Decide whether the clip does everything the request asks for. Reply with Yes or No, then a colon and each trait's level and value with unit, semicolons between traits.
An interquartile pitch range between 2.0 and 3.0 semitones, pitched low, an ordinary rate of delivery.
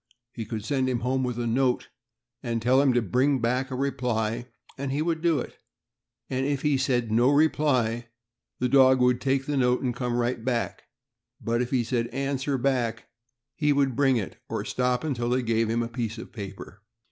Yes: narrow, 2.5 semitones; low, 125 Hz; average, 195 wpm